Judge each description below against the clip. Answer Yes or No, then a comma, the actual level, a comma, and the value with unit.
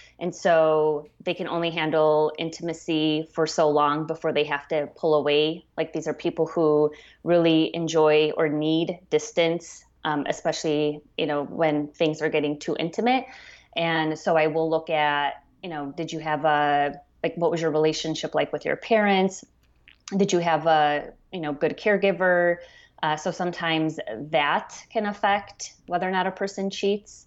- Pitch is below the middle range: No, medium, 160 Hz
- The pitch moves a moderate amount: No, narrow, 2.3 semitones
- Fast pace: No, average, 170 wpm